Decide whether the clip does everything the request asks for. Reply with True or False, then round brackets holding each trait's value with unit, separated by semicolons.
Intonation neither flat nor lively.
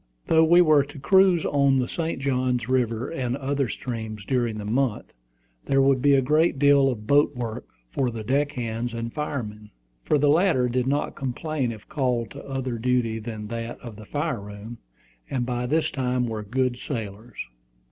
True (3.5 semitones)